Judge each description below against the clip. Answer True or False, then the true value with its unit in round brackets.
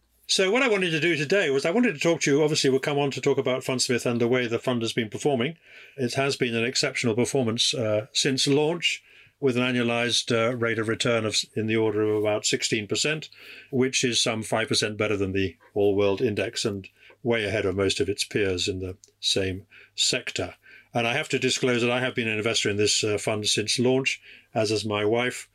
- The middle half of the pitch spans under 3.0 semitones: False (3.9 semitones)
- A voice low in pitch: True (120 Hz)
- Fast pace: True (225 wpm)